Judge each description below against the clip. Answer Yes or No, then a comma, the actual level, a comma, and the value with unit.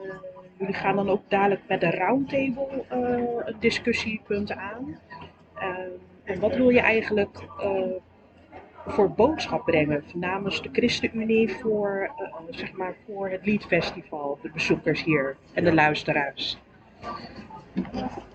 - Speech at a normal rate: No, slow, 130 wpm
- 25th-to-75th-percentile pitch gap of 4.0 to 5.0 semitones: Yes, average, 4.3 semitones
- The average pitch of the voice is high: Yes, high, 195 Hz